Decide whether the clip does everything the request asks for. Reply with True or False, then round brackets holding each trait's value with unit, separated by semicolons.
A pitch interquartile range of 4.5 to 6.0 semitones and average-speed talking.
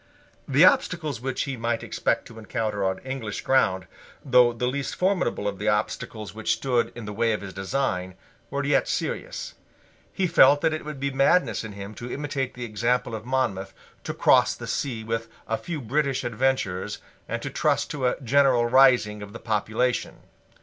False (4.1 semitones; 185 wpm)